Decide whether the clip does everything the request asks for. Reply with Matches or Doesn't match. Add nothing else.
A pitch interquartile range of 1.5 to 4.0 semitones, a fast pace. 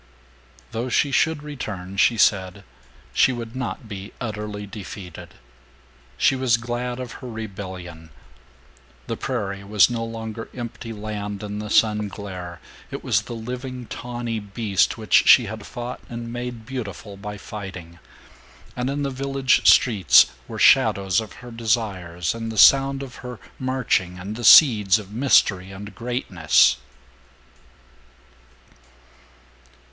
Doesn't match